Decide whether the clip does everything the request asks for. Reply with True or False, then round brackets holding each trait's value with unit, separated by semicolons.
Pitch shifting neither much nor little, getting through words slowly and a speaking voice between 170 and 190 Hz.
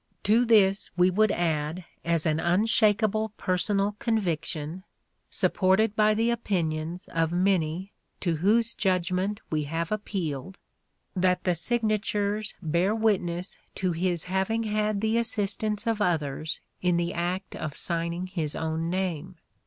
True (3.9 semitones; 130 wpm; 185 Hz)